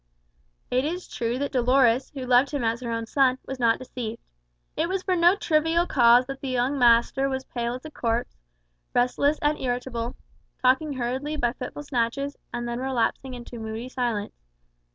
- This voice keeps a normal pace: Yes, average, 175 wpm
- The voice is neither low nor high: No, very high, 255 Hz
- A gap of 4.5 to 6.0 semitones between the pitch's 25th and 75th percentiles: No, average, 2.8 semitones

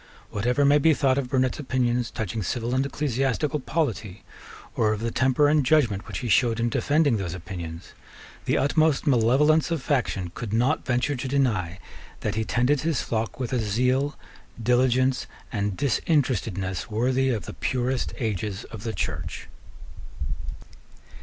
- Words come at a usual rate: Yes, average, 155 wpm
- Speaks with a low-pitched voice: Yes, low, 125 Hz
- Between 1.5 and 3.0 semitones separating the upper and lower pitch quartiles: No, average, 4.0 semitones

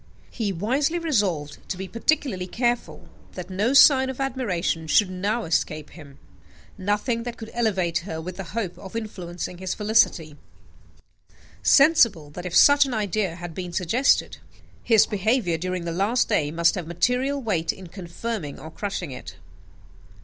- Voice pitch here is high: Yes, high, 195 Hz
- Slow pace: No, average, 155 wpm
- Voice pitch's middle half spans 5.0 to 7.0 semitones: Yes, average, 5.3 semitones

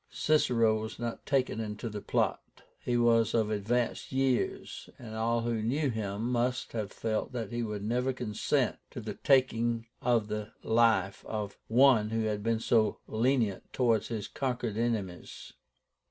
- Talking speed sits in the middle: Yes, average, 155 wpm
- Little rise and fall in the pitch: Yes, narrow, 2.1 semitones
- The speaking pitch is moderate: No, low, 115 Hz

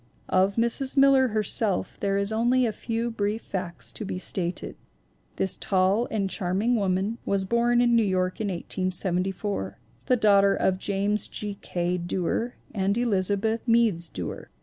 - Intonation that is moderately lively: Yes, average, 3.6 semitones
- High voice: Yes, high, 200 Hz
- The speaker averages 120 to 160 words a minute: Yes, average, 150 wpm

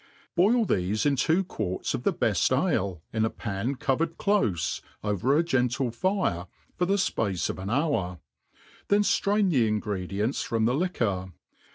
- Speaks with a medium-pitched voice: No, low, 120 Hz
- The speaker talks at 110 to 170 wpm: Yes, average, 165 wpm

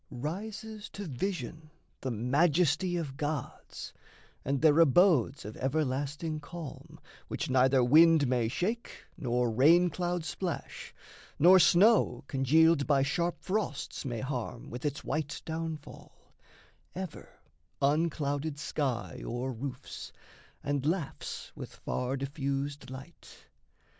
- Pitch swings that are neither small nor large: Yes, average, 4.0 semitones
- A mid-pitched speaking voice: Yes, medium, 145 Hz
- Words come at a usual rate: No, slow, 115 wpm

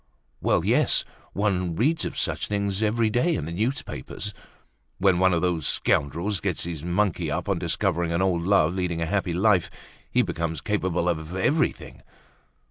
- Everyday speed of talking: Yes, average, 165 wpm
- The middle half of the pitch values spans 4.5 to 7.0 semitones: No, average, 3.5 semitones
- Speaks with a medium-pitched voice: No, very low, 90 Hz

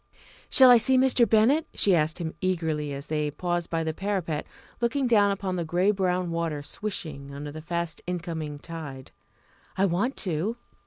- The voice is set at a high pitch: No, medium, 175 Hz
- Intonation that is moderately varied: Yes, average, 4.5 semitones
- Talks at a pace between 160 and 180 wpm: Yes, average, 170 wpm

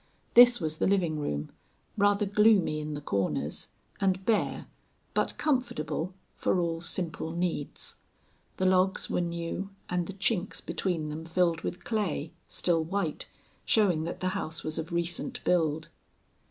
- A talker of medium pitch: Yes, medium, 175 Hz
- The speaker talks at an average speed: Yes, average, 145 wpm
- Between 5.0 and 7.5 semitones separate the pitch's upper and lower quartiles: No, average, 3.6 semitones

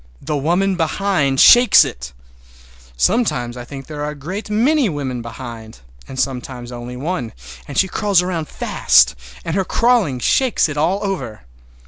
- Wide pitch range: Yes, wide, 7.6 semitones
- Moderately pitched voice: Yes, medium, 150 Hz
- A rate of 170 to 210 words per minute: No, average, 155 wpm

